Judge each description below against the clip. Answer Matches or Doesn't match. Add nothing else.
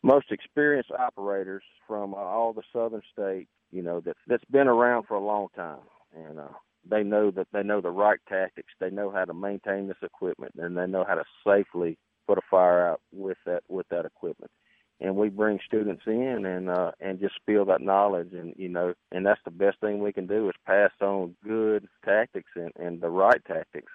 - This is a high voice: Doesn't match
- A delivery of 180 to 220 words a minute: Matches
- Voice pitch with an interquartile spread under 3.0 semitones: Matches